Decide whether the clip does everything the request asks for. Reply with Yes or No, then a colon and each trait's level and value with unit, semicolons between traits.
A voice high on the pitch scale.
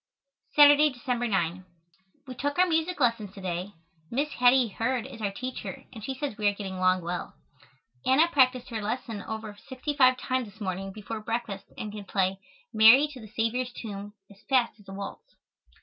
Yes: high, 230 Hz